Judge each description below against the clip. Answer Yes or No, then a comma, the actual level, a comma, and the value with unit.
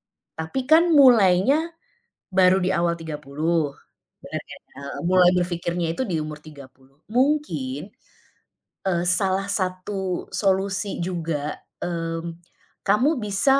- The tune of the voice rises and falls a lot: No, average, 3.3 semitones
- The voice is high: No, medium, 175 Hz